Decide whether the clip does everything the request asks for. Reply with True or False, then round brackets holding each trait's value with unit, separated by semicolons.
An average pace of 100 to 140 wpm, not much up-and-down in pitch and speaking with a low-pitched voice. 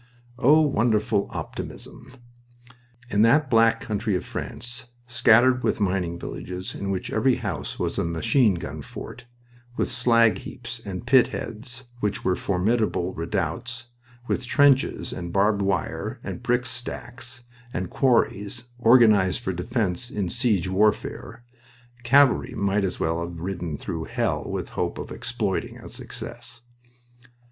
False (135 wpm; 4.5 semitones; 110 Hz)